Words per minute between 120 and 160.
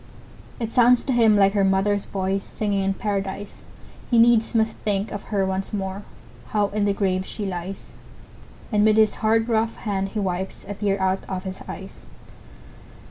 No: average, 180 wpm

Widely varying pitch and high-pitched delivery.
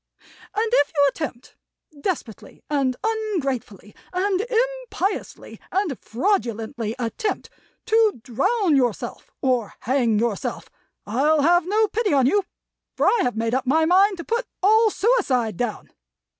Yes: wide, 9.0 semitones; very high, 305 Hz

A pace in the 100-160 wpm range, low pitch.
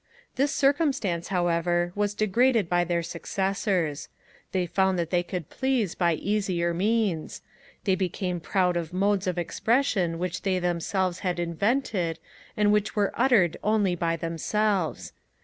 No: average, 140 wpm; medium, 185 Hz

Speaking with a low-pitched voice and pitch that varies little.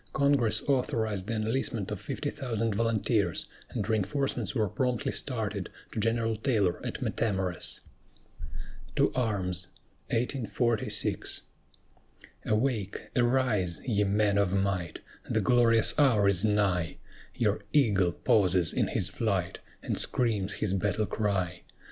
No: low, 105 Hz; average, 3.2 semitones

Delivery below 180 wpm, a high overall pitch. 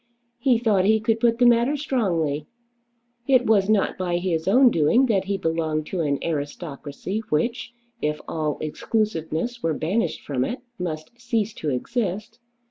Yes: average, 155 wpm; high, 195 Hz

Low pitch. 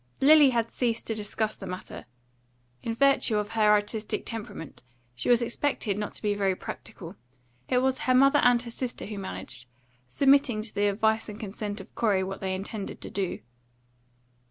No: high, 220 Hz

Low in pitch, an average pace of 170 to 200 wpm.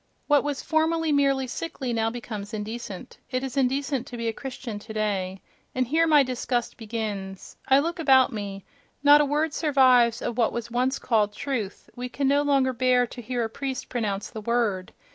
No: very high, 250 Hz; average, 180 wpm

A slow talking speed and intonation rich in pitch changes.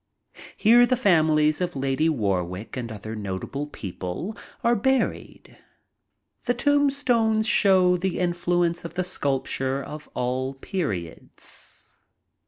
Yes: slow, 110 wpm; wide, 7.8 semitones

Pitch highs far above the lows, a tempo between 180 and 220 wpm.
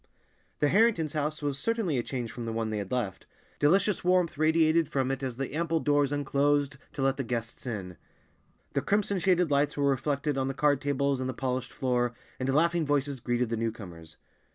No: average, 3.8 semitones; average, 200 wpm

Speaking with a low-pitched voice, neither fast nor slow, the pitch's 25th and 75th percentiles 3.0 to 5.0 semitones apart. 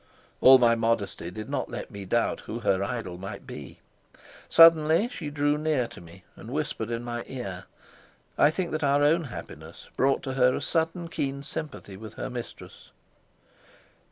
No: low, 130 Hz; average, 170 wpm; wide, 5.6 semitones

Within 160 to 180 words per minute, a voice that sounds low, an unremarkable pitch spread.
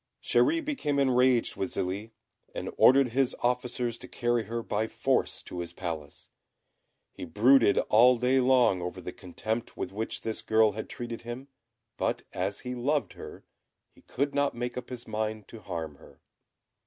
Yes: average, 165 wpm; low, 120 Hz; average, 3.6 semitones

